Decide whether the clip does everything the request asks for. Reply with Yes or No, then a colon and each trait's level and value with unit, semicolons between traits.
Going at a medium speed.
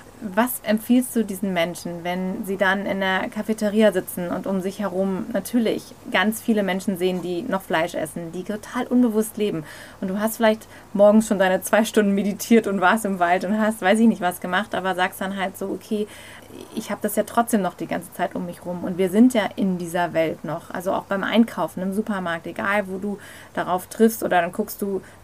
No: fast, 215 wpm